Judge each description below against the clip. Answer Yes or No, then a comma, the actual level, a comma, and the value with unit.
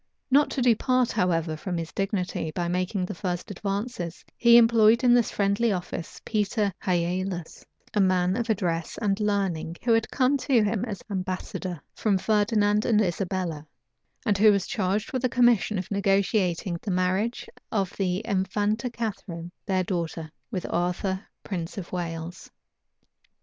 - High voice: Yes, high, 195 Hz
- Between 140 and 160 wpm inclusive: Yes, average, 150 wpm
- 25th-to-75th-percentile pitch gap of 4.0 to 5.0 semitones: No, average, 3.4 semitones